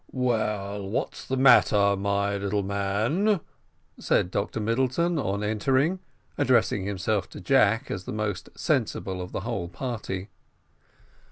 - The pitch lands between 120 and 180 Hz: No, low, 105 Hz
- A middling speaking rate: No, slow, 125 wpm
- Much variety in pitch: No, average, 4.3 semitones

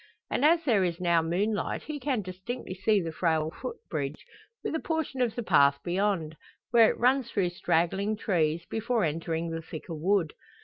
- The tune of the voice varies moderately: No, wide, 5.9 semitones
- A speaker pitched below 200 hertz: Yes, medium, 185 Hz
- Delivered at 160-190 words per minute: Yes, average, 175 wpm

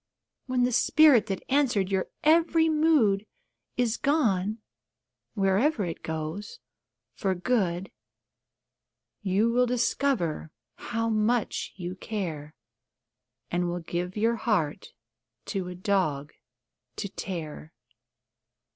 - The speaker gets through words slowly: Yes, slow, 100 wpm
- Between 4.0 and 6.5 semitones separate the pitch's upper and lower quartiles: Yes, wide, 5.5 semitones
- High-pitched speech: Yes, high, 200 Hz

